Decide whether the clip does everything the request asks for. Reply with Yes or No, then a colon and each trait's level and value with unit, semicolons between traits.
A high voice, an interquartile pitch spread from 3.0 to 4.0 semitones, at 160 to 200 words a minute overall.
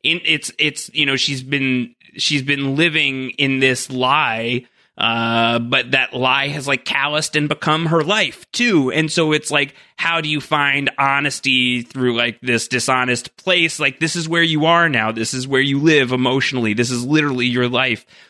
No: low, 135 Hz; average, 3.4 semitones; average, 185 wpm